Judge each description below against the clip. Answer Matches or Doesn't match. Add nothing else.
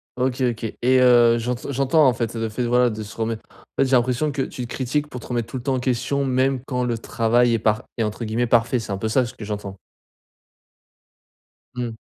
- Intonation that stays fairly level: Matches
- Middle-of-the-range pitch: Doesn't match